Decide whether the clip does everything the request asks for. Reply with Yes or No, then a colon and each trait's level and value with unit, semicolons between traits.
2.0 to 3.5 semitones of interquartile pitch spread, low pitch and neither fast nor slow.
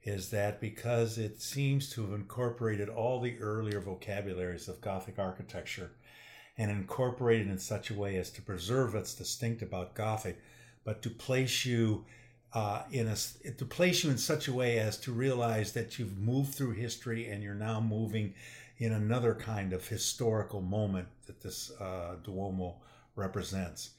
Yes: average, 2.8 semitones; low, 110 Hz; average, 165 wpm